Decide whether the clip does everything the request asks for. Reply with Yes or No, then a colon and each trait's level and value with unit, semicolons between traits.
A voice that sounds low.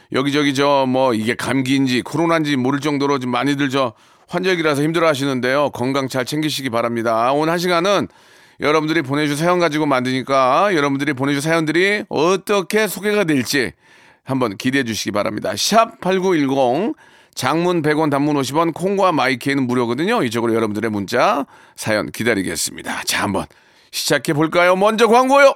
No: medium, 145 Hz